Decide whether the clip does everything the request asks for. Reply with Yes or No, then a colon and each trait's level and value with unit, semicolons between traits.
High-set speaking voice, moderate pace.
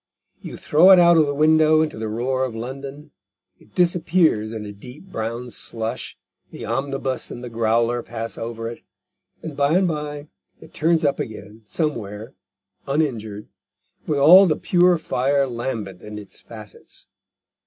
No: low, 130 Hz; average, 155 wpm